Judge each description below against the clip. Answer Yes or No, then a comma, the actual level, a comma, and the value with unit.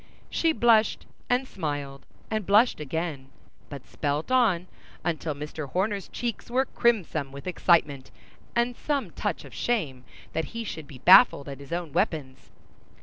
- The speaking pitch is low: No, medium, 170 Hz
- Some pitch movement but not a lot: No, wide, 7.9 semitones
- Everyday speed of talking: Yes, average, 145 wpm